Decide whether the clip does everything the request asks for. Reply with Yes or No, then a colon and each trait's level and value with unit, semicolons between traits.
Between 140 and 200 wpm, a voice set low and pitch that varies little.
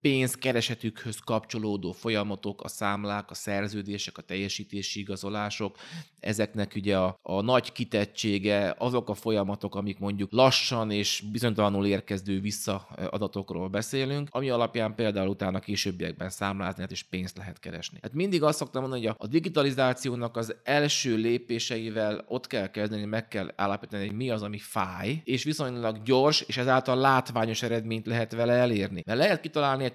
No: average, 150 wpm; low, 110 Hz; average, 3.6 semitones